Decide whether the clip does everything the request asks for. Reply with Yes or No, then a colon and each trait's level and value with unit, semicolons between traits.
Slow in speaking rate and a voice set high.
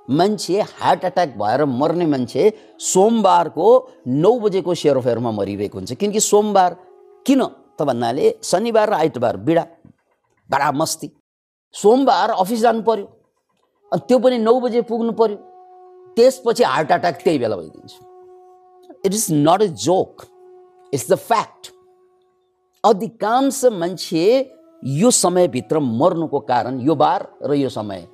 Yes: slow, 125 wpm; high, 215 Hz